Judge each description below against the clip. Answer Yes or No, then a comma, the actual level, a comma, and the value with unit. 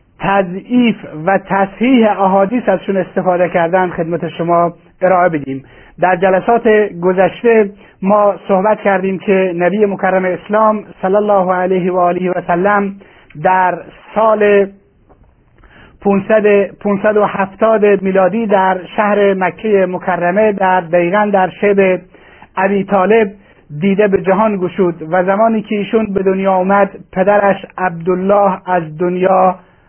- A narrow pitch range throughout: Yes, narrow, 2.1 semitones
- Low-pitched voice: No, high, 190 Hz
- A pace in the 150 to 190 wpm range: No, average, 115 wpm